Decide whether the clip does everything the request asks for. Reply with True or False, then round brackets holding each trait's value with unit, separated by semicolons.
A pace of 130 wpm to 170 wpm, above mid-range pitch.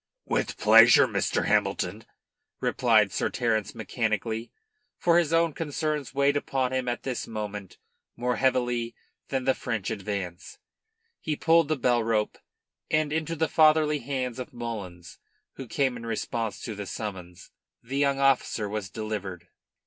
False (145 wpm; 125 Hz)